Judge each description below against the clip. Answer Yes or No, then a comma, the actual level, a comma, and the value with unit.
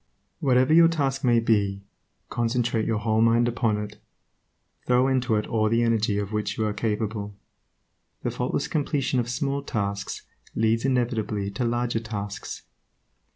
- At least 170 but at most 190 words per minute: No, average, 150 wpm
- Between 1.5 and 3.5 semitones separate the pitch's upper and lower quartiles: Yes, average, 3.0 semitones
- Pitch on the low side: Yes, low, 115 Hz